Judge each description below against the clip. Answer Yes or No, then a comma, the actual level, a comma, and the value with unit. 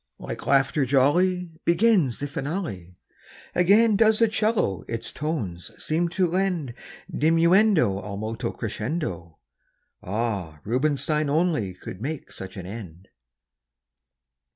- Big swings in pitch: Yes, wide, 9.0 semitones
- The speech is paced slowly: Yes, slow, 110 wpm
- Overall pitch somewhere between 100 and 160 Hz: Yes, medium, 140 Hz